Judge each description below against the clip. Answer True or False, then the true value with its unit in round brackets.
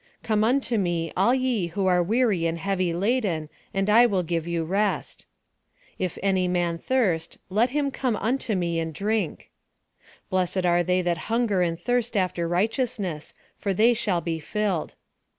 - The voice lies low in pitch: False (190 Hz)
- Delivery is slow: False (175 wpm)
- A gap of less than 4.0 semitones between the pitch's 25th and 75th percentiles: False (4.6 semitones)